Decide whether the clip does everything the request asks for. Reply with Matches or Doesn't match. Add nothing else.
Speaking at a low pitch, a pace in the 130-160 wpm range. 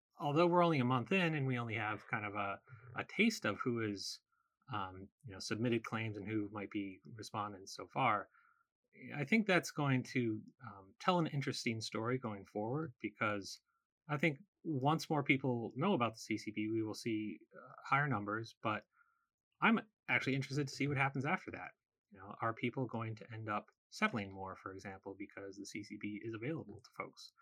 Doesn't match